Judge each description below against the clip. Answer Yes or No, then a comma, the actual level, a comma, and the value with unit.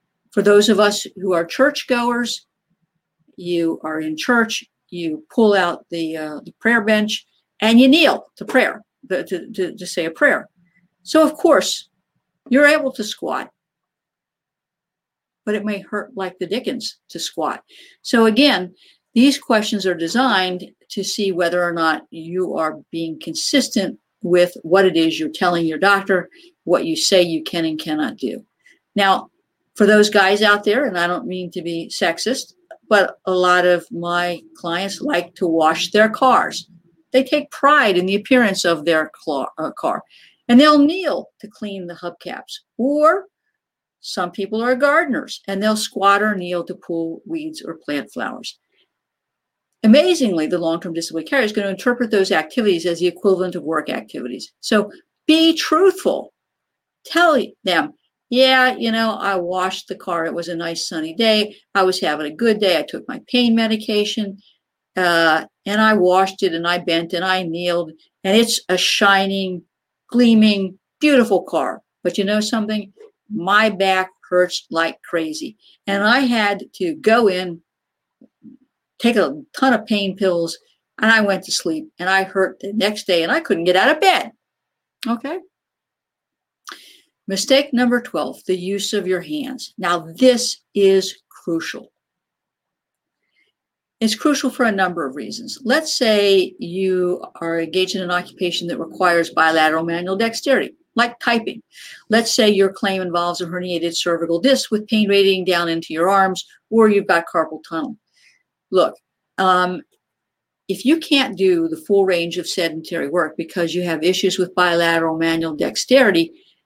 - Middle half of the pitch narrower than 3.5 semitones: No, average, 5.0 semitones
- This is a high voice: Yes, high, 195 Hz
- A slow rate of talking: No, average, 160 wpm